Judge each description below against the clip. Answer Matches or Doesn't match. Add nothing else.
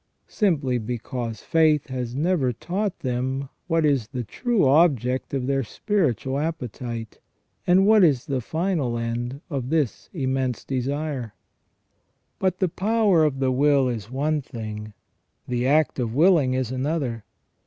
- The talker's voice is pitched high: Doesn't match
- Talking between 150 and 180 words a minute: Doesn't match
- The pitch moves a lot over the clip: Doesn't match